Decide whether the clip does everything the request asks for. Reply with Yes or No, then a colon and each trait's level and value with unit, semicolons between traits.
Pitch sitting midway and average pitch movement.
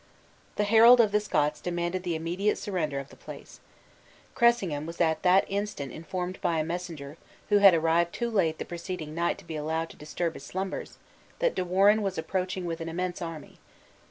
Yes: medium, 175 Hz; average, 3.3 semitones